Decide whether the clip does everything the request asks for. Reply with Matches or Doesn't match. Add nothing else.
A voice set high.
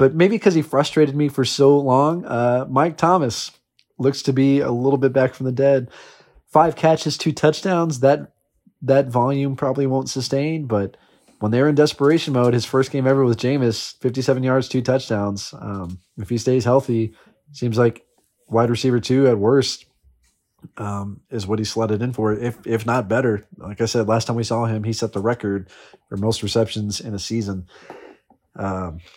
Doesn't match